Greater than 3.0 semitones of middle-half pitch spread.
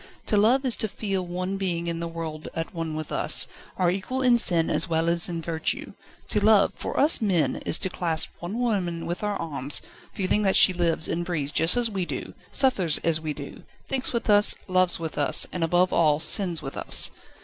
Yes: average, 3.7 semitones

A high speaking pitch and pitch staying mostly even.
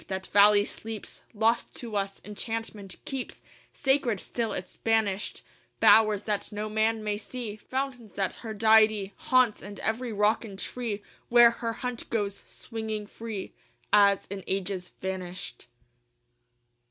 Yes: high, 215 Hz; narrow, 2.2 semitones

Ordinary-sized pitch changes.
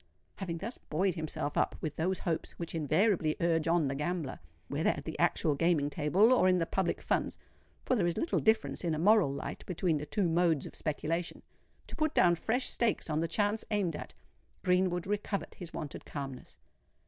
Yes: average, 3.8 semitones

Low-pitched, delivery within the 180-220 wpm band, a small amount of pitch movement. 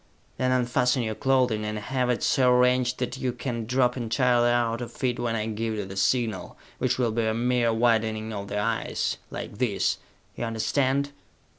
Yes: low, 120 Hz; average, 185 wpm; narrow, 2.2 semitones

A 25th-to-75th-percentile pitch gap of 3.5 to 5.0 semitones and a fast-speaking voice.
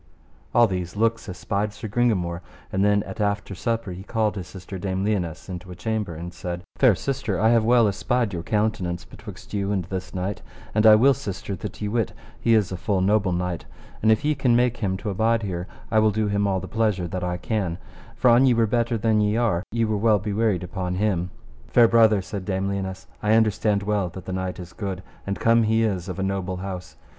No: average, 3.1 semitones; fast, 225 wpm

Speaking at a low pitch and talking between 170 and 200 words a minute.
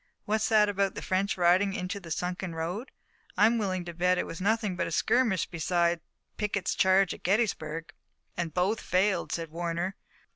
No: medium, 185 Hz; average, 175 wpm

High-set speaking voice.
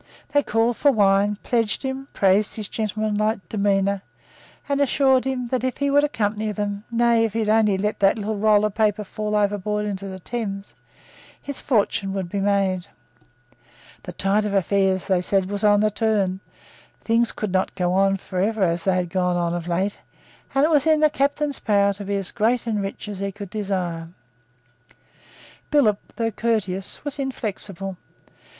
Yes: high, 210 Hz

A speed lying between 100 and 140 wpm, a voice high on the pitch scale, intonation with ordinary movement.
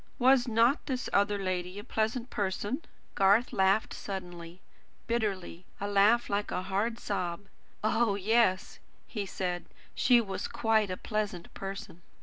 Yes: slow, 135 wpm; high, 205 Hz; average, 3.2 semitones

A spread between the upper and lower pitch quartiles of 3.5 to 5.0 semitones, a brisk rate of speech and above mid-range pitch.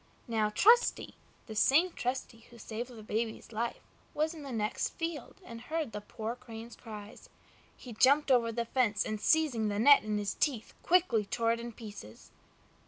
No: average, 4.0 semitones; average, 175 wpm; high, 235 Hz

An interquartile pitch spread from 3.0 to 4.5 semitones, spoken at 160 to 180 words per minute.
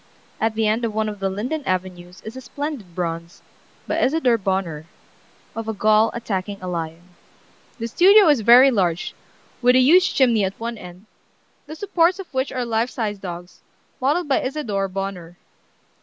No: wide, 5.6 semitones; average, 170 wpm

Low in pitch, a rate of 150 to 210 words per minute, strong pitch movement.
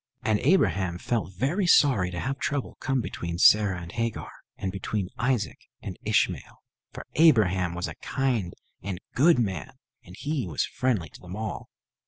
Yes: low, 105 Hz; average, 165 wpm; wide, 6.4 semitones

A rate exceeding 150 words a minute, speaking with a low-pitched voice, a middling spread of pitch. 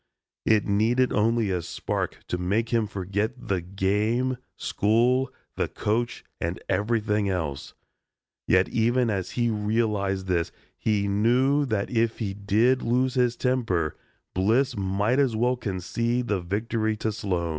No: average, 140 wpm; low, 110 Hz; average, 3.4 semitones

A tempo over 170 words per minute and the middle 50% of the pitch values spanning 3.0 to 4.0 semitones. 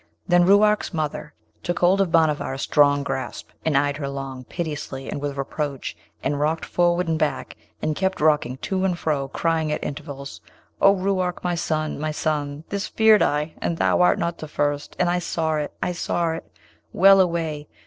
Yes: average, 190 wpm; average, 3.4 semitones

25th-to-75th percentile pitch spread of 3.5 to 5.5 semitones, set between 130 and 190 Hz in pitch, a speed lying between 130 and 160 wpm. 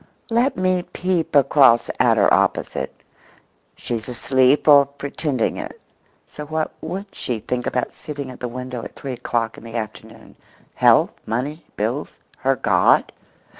Yes: average, 3.8 semitones; low, 135 Hz; average, 145 wpm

